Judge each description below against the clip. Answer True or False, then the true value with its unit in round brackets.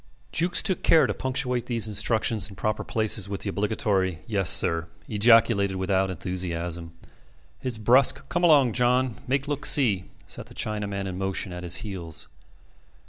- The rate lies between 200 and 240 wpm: False (155 wpm)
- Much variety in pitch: False (4.8 semitones)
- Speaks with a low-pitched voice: True (105 Hz)